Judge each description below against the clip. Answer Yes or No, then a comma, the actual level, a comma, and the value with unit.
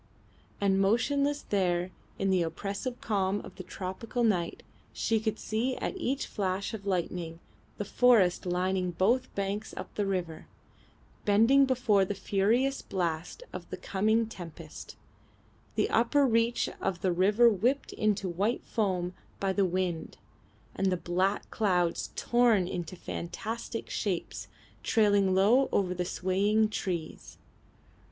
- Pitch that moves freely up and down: No, average, 3.6 semitones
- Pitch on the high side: Yes, high, 195 Hz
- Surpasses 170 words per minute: No, slow, 135 wpm